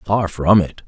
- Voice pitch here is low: Yes, very low, 95 Hz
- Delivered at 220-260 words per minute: No, fast, 205 wpm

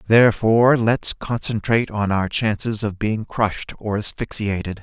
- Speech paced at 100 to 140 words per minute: Yes, slow, 135 wpm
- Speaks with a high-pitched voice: No, low, 110 Hz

